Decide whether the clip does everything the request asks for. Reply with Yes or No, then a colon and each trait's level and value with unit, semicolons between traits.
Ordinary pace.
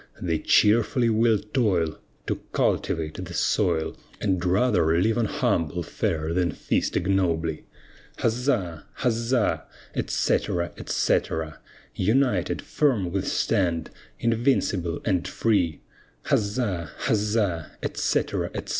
No: slow, 100 wpm